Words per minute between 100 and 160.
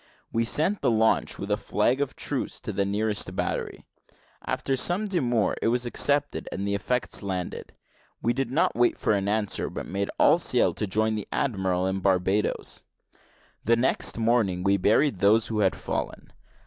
No: average, 175 wpm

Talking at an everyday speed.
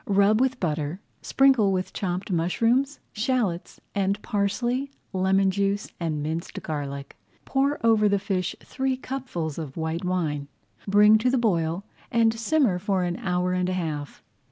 Yes: average, 150 wpm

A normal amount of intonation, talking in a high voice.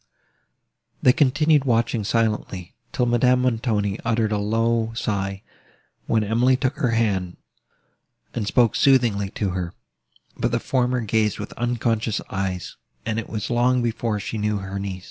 No: average, 3.0 semitones; low, 115 Hz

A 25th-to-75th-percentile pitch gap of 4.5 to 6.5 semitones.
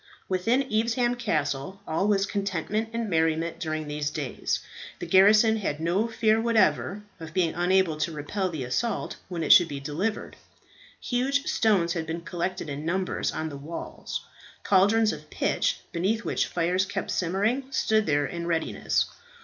Yes: average, 5.2 semitones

